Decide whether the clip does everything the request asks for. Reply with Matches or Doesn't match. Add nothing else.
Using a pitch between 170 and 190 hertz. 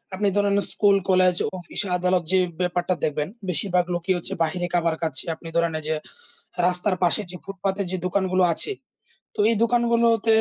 Matches